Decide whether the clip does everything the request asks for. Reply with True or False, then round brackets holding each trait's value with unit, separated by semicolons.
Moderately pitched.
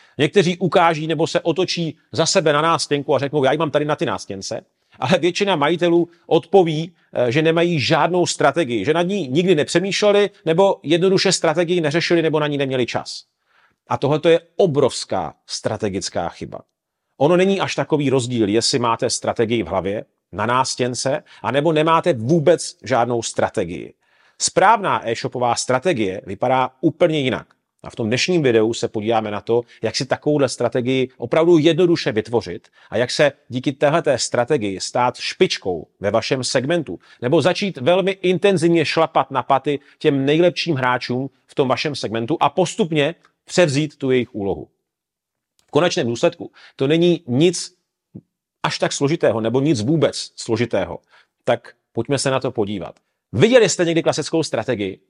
True (150 Hz)